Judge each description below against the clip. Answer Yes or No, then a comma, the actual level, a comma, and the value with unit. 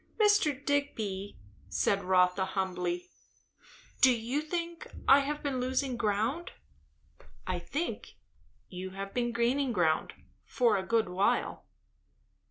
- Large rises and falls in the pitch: Yes, wide, 6.8 semitones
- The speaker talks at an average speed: No, slow, 115 wpm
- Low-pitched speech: No, high, 235 Hz